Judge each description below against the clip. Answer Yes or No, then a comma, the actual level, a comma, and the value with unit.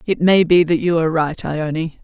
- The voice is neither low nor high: Yes, medium, 165 Hz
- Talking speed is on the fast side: Yes, fast, 235 wpm